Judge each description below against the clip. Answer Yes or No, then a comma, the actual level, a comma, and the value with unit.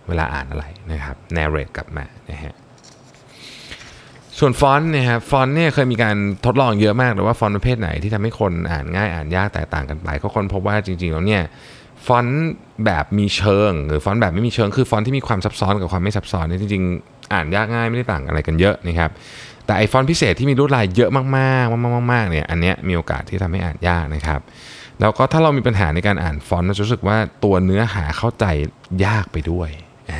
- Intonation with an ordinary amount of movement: No, wide, 5.9 semitones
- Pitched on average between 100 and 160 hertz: Yes, low, 105 Hz